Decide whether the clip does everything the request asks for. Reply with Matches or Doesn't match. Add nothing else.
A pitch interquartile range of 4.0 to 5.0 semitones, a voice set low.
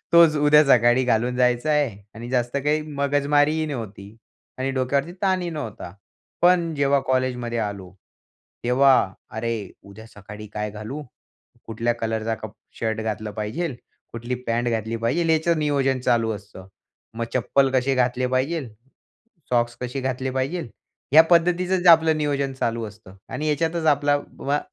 Matches